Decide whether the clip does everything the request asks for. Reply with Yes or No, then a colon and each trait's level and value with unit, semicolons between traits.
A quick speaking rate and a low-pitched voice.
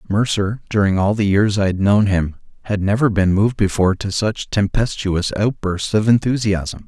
No: average, 175 wpm; low, 100 Hz